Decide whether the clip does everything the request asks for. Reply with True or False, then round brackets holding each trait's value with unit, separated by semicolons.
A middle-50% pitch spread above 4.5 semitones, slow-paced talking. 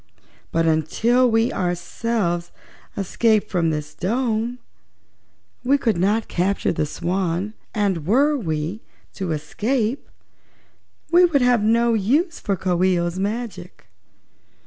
True (5.3 semitones; 120 wpm)